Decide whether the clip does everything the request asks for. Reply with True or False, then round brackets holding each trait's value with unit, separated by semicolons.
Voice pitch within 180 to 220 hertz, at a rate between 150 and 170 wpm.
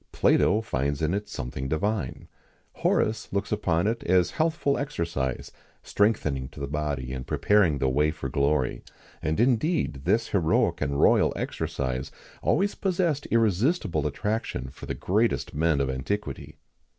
False (85 Hz; 160 wpm)